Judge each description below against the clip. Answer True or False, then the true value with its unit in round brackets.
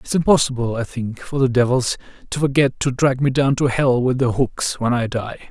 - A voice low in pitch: True (125 Hz)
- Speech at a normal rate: False (230 wpm)